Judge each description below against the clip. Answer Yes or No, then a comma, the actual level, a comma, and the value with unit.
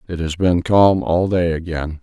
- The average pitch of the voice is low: Yes, very low, 85 Hz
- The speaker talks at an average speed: No, fast, 210 wpm